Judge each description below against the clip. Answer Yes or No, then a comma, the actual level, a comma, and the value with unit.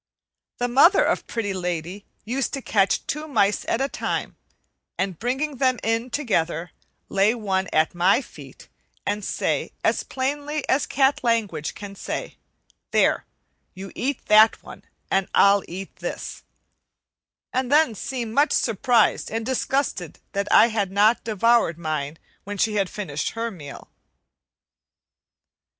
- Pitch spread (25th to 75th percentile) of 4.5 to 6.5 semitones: Yes, average, 4.8 semitones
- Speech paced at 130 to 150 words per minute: Yes, average, 140 wpm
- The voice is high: Yes, high, 220 Hz